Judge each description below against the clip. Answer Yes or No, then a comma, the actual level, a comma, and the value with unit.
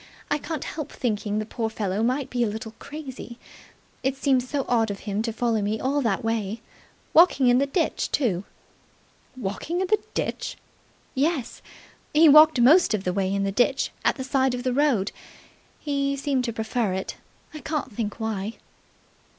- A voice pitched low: No, high, 245 Hz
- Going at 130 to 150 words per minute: No, average, 180 wpm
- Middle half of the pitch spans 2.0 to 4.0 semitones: No, average, 4.5 semitones